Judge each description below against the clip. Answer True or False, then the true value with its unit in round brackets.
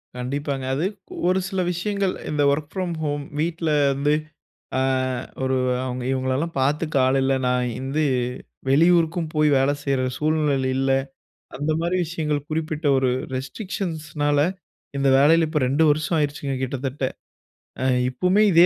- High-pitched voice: False (150 Hz)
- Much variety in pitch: False (3.4 semitones)